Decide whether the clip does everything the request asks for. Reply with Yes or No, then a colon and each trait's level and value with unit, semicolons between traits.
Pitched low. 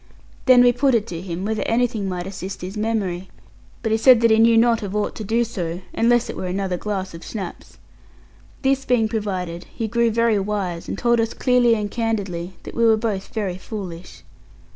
No: high, 215 Hz